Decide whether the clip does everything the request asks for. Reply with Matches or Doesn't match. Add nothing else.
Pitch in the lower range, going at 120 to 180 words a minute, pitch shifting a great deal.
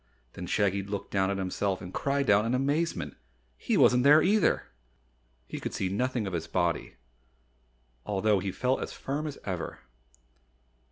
Matches